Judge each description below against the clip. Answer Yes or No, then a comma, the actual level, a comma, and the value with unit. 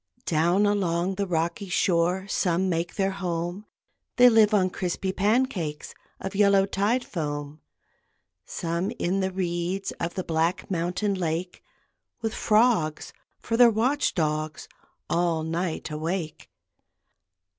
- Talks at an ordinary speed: No, slow, 125 wpm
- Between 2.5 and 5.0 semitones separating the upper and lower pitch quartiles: Yes, average, 3.1 semitones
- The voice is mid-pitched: Yes, medium, 180 Hz